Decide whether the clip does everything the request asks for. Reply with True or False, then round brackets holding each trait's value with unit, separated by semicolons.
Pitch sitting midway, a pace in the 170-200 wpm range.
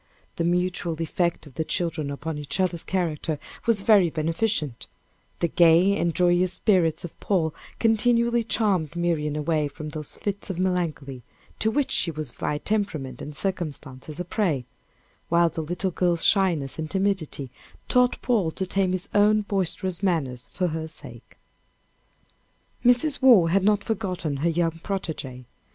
False (175 Hz; 150 wpm)